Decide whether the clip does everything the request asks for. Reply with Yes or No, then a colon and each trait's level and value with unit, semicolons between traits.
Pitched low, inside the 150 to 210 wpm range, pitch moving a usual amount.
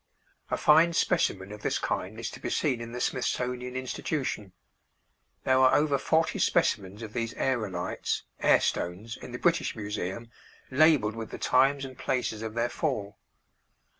Yes: low, 120 Hz; average, 160 wpm; average, 3.9 semitones